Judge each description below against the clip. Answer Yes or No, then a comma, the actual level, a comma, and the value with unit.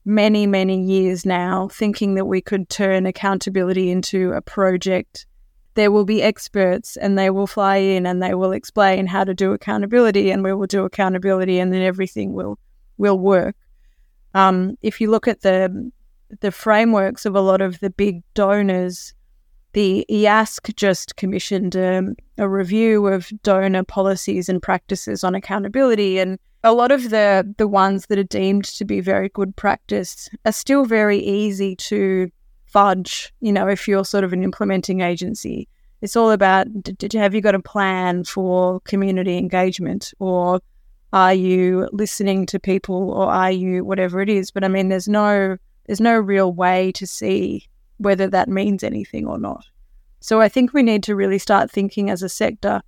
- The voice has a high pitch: Yes, high, 195 Hz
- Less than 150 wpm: No, average, 175 wpm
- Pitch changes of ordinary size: No, narrow, 1.6 semitones